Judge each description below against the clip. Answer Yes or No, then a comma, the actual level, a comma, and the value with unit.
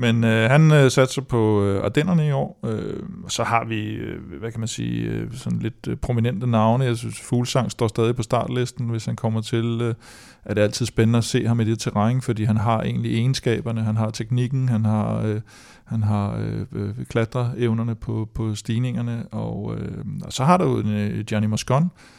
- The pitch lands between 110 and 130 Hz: Yes, low, 115 Hz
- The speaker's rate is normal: Yes, average, 200 wpm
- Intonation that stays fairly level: Yes, narrow, 2.2 semitones